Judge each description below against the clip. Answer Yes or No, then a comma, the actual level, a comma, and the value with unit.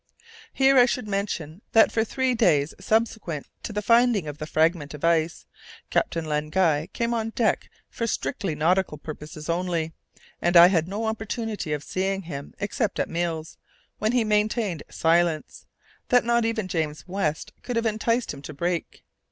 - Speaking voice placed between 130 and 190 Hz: Yes, medium, 185 Hz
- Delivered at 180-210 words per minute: No, average, 170 wpm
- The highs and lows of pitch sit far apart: Yes, wide, 5.8 semitones